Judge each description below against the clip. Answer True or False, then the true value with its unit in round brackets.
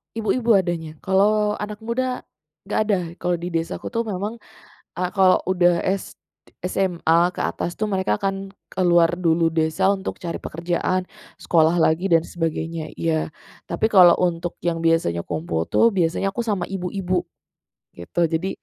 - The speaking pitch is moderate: True (180 Hz)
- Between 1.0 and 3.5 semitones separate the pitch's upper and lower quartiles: True (2.9 semitones)